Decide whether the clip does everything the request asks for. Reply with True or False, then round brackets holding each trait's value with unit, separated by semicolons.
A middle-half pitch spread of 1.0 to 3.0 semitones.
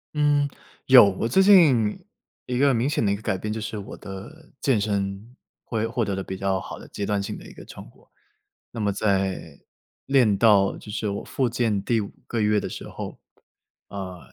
False (3.7 semitones)